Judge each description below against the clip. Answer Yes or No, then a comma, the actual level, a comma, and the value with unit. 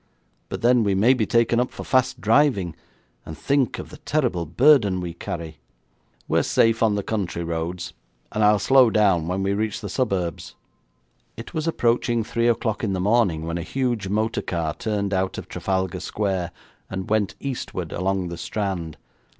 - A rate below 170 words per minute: No, average, 175 wpm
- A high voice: No, low, 100 Hz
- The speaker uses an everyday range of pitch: Yes, average, 4.6 semitones